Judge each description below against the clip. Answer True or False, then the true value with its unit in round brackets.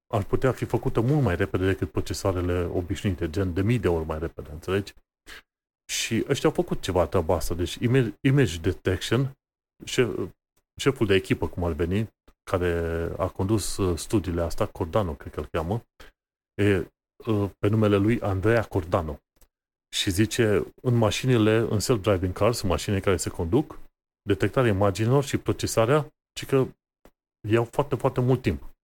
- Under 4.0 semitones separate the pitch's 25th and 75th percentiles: False (4.5 semitones)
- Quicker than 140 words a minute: True (150 wpm)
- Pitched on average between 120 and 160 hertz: False (100 Hz)